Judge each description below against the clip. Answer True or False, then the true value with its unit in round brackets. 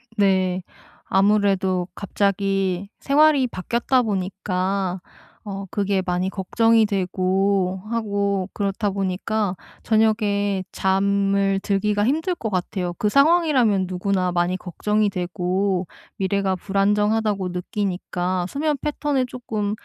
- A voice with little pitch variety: True (2.2 semitones)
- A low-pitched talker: False (200 Hz)